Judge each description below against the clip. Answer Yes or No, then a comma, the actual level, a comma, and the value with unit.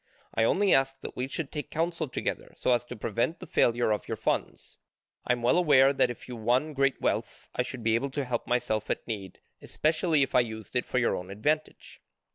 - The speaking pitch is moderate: No, low, 125 Hz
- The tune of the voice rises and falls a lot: No, average, 4.0 semitones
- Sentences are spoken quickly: Yes, fast, 225 wpm